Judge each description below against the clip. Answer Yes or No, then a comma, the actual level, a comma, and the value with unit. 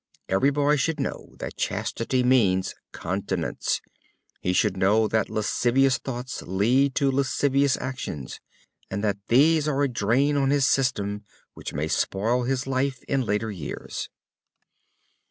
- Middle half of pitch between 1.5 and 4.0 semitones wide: No, average, 5.0 semitones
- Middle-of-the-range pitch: No, low, 125 Hz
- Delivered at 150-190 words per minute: No, slow, 135 wpm